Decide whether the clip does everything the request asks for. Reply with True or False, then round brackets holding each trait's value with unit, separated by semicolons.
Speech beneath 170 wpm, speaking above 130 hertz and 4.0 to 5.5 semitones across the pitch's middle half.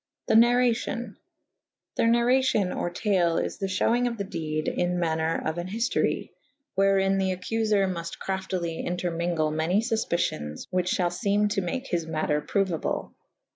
True (150 wpm; 190 Hz; 4.4 semitones)